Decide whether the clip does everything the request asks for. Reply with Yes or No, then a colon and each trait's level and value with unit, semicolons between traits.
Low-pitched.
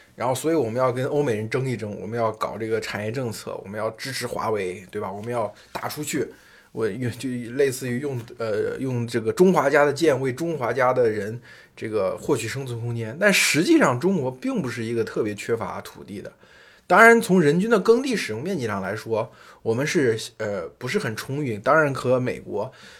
Yes: low, 130 Hz